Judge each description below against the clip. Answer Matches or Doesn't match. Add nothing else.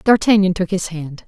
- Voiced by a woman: Matches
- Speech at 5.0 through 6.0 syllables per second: Matches